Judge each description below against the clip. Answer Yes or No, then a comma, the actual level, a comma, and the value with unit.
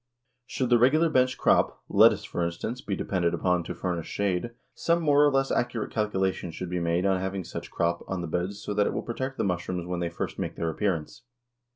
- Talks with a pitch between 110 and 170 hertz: No, very low, 95 Hz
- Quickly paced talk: Yes, fast, 220 wpm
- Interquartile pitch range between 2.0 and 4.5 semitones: No, wide, 5.6 semitones